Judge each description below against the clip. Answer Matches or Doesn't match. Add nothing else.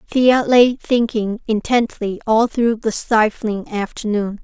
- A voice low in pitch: Doesn't match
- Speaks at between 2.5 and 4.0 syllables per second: Matches